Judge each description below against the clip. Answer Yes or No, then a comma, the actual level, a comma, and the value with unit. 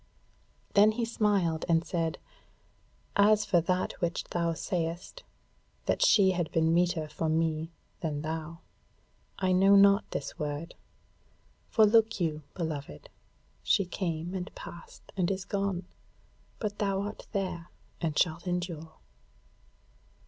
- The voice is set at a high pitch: No, medium, 175 Hz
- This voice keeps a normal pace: No, slow, 125 wpm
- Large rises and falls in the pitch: No, average, 3.3 semitones